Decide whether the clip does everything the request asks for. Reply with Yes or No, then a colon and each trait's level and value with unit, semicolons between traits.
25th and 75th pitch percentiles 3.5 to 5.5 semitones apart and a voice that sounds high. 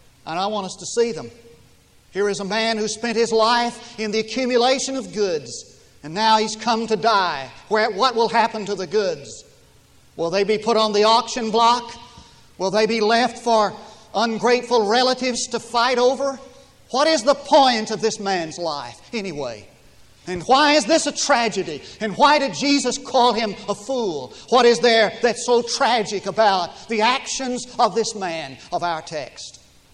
No: average, 3.1 semitones; high, 230 Hz